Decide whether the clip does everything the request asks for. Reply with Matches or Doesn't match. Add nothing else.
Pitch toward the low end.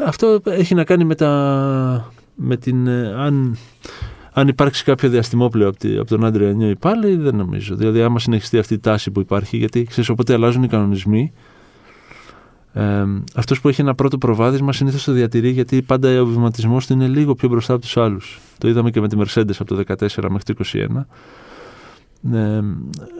Matches